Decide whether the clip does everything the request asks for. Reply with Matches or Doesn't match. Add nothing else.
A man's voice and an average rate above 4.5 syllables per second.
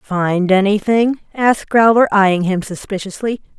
Doesn't match